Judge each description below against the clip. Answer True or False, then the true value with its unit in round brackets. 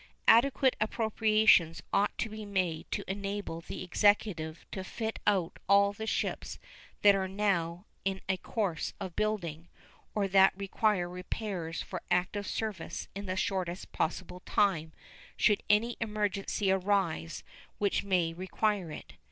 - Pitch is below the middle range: False (195 Hz)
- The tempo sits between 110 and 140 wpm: True (135 wpm)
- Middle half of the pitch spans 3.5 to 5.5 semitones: False (2.8 semitones)